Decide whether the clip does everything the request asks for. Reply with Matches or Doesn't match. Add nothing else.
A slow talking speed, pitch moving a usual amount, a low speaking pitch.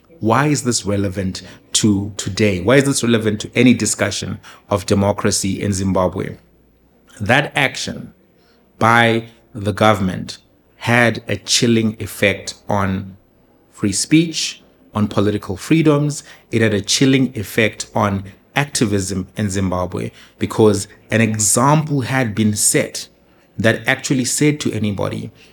Matches